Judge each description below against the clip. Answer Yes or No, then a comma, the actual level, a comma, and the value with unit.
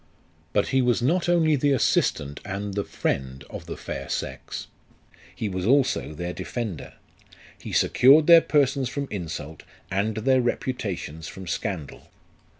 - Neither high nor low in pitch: No, low, 110 Hz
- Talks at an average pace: Yes, average, 150 wpm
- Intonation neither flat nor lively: No, wide, 7.2 semitones